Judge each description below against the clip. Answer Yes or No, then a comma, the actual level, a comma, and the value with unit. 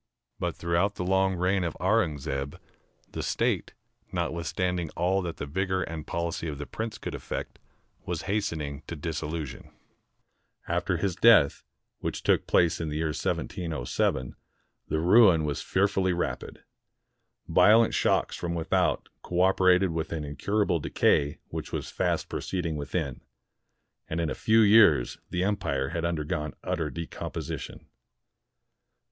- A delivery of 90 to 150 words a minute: Yes, average, 140 wpm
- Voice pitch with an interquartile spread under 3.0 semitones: No, average, 3.7 semitones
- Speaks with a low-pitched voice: Yes, very low, 85 Hz